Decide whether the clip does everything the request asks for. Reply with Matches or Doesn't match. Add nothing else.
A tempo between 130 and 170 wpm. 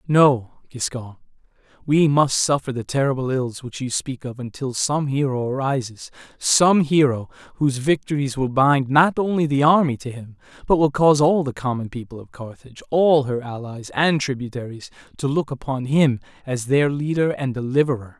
Matches